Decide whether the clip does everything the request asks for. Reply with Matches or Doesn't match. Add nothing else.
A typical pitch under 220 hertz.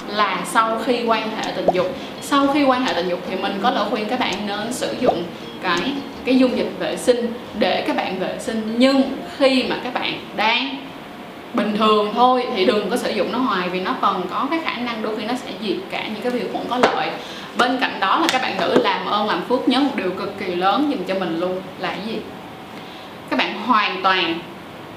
Doesn't match